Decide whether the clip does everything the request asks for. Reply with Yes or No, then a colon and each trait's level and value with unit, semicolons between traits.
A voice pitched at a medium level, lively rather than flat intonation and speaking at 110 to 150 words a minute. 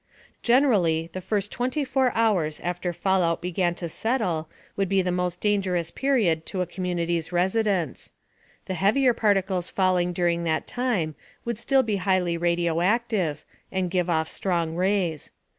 No: medium, 180 Hz; average, 3.3 semitones; average, 140 wpm